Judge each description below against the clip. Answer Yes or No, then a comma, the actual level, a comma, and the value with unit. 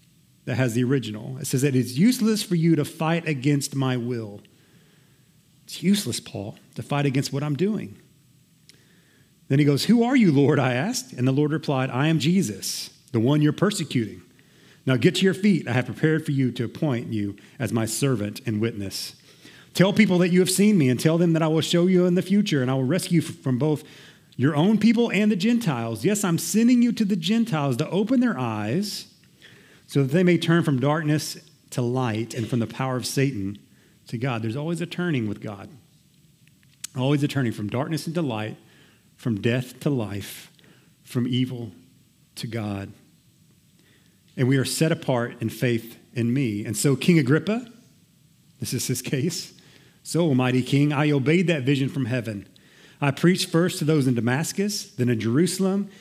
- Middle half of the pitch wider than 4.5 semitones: Yes, average, 5.2 semitones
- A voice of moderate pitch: Yes, medium, 145 Hz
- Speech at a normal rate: Yes, average, 190 wpm